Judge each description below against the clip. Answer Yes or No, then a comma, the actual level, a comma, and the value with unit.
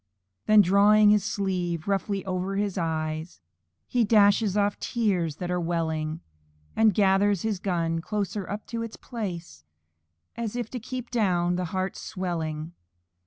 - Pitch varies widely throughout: No, average, 3.4 semitones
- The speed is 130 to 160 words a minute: Yes, average, 145 wpm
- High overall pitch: Yes, high, 195 Hz